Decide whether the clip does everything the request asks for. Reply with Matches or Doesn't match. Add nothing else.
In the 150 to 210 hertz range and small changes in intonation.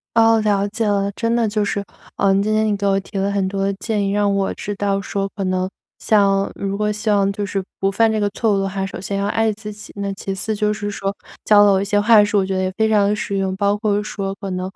Matches